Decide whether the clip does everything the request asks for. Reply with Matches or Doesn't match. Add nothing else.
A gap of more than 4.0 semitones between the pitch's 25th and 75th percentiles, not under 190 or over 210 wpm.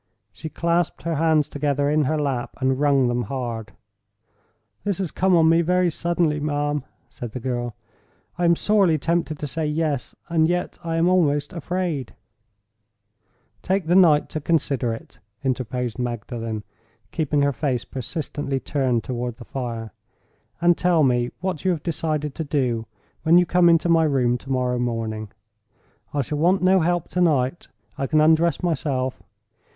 Doesn't match